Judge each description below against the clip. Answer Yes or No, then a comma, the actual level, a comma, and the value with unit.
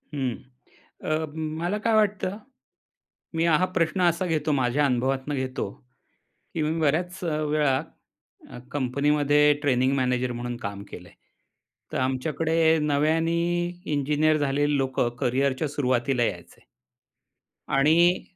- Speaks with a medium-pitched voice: Yes, medium, 145 Hz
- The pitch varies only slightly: No, average, 3.7 semitones